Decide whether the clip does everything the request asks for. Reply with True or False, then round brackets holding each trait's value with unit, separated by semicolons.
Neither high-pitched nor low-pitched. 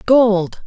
False (215 Hz)